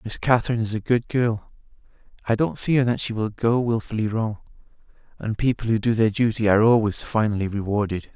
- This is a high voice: No, low, 110 Hz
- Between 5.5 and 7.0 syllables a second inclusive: Yes, 5.8 syllables/s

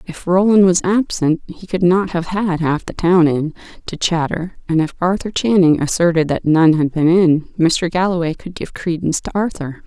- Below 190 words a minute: No, average, 195 wpm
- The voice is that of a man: No, female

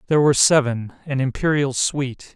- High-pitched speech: No, low, 135 Hz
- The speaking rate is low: Yes, slow, 130 wpm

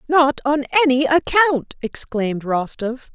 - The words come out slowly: Yes, slow, 115 wpm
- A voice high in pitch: Yes, very high, 270 Hz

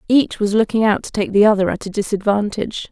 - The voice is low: No, high, 210 Hz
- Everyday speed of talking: No, fast, 225 wpm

